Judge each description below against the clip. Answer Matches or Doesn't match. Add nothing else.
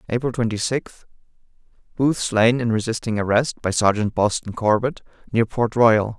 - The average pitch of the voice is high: Doesn't match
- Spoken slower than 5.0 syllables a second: Matches